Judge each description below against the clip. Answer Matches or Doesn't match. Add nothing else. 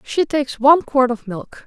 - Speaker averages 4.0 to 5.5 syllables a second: Matches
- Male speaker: Doesn't match